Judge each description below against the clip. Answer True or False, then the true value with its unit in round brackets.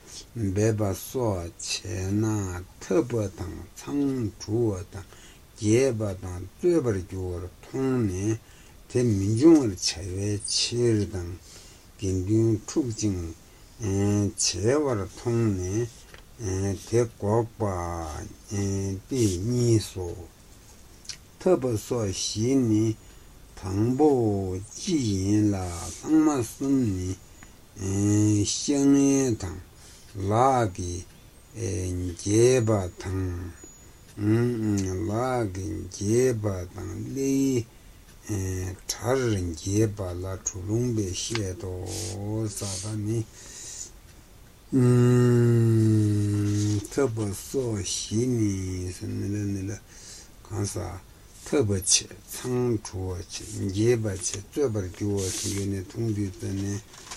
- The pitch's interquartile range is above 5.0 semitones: False (3.4 semitones)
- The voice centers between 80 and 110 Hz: True (105 Hz)